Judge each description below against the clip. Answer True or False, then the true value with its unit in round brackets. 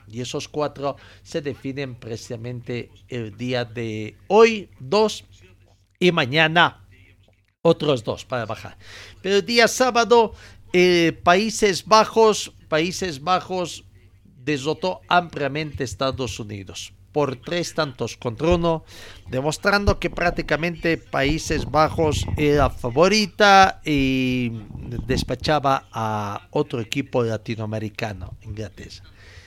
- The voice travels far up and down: True (7.7 semitones)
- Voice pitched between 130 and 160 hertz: True (135 Hz)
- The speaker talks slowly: True (100 wpm)